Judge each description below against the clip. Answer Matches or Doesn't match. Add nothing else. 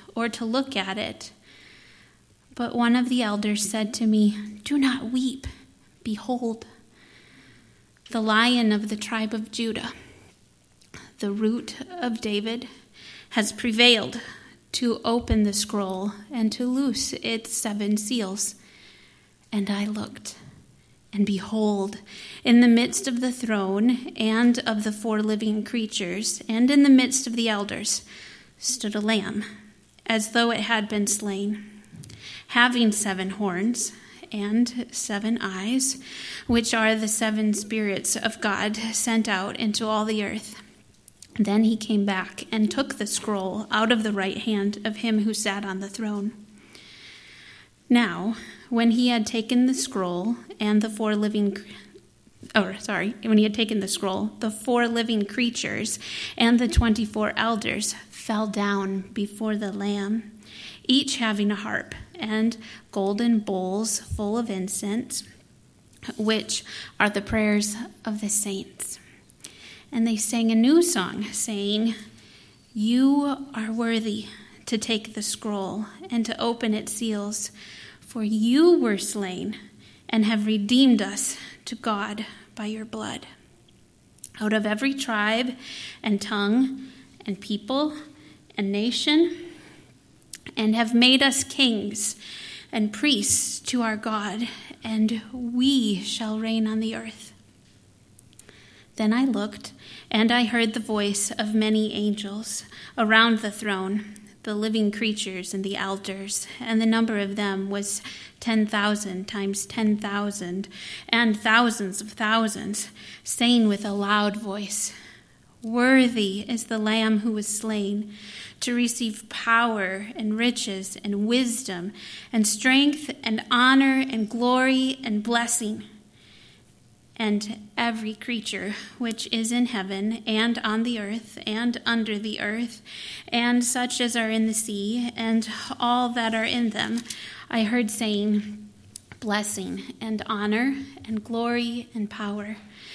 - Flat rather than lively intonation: Matches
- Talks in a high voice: Matches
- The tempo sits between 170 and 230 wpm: Doesn't match